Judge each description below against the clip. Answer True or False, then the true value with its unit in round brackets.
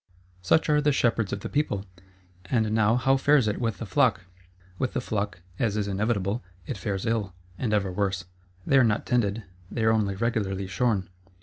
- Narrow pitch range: False (3.4 semitones)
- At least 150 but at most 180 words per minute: False (190 wpm)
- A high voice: False (110 Hz)